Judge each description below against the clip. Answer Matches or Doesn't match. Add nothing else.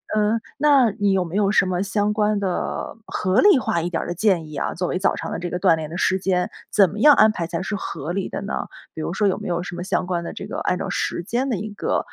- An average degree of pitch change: Matches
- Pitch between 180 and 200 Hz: Matches